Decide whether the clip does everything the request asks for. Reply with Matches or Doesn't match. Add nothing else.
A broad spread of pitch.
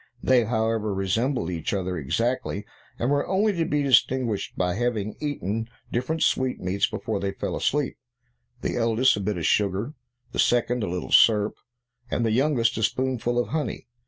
Doesn't match